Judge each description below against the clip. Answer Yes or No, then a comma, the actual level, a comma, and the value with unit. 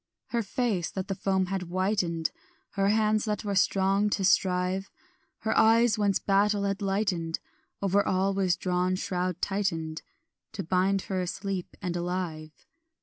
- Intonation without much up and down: Yes, narrow, 1.9 semitones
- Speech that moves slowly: No, average, 150 wpm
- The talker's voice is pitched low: No, high, 195 Hz